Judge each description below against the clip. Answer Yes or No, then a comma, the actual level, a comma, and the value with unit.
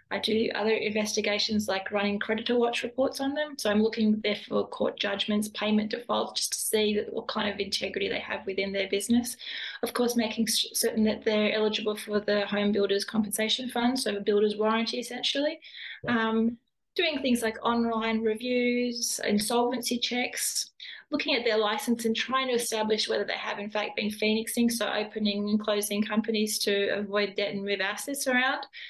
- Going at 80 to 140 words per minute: No, average, 180 wpm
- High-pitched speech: Yes, high, 220 Hz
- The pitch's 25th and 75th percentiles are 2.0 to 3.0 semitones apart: Yes, narrow, 2.4 semitones